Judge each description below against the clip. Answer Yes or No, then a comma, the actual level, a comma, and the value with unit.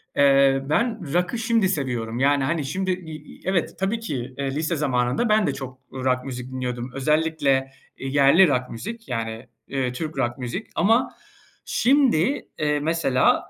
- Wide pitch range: Yes, wide, 5.7 semitones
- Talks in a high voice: No, medium, 145 Hz